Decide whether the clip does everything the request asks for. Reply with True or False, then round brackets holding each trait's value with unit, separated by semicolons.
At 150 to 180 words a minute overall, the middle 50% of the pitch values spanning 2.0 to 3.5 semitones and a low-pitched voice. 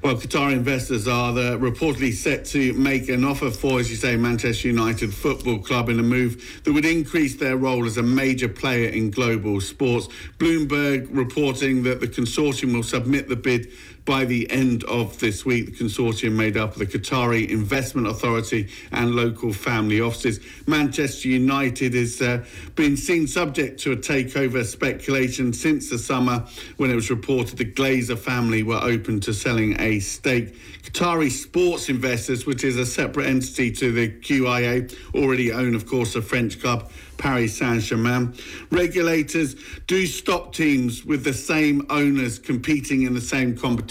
True (165 wpm; 2.6 semitones; 125 Hz)